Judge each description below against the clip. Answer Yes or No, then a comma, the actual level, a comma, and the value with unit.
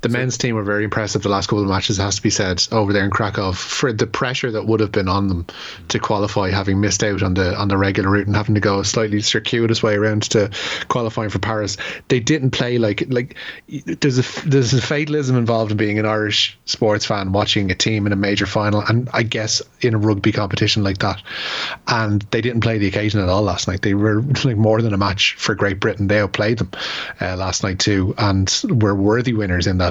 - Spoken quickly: Yes, fast, 240 wpm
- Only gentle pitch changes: Yes, narrow, 2.3 semitones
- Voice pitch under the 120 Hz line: Yes, low, 105 Hz